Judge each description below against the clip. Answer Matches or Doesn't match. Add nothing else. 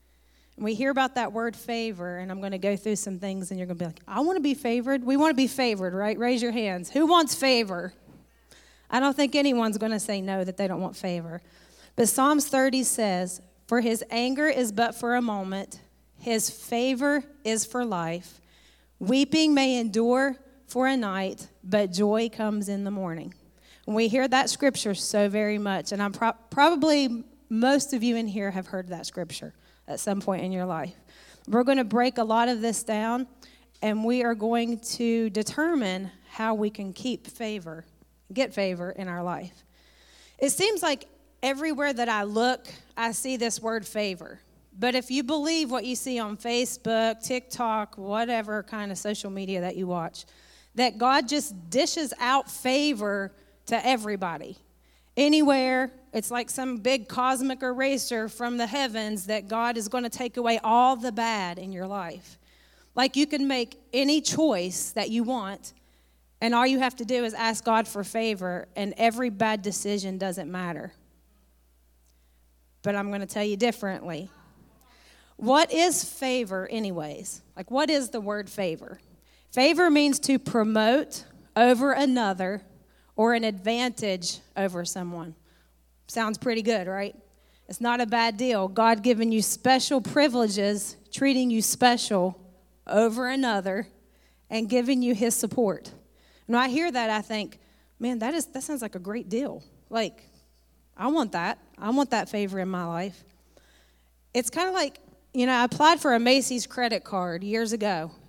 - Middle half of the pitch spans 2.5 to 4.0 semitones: Doesn't match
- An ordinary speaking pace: Matches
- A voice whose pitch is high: Matches